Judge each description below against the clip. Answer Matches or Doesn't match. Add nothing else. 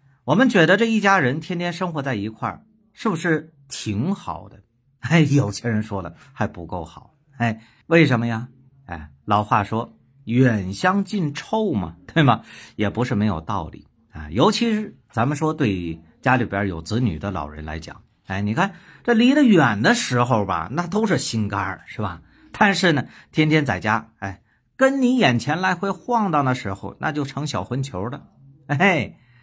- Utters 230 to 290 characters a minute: Matches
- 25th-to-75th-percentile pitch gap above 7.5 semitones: Matches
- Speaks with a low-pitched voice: Matches